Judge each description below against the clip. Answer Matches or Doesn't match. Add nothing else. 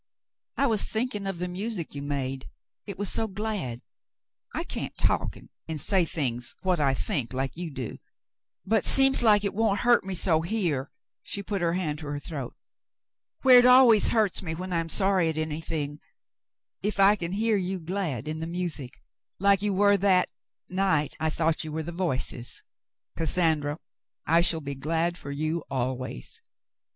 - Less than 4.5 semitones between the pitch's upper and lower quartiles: Doesn't match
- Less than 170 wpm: Doesn't match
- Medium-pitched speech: Matches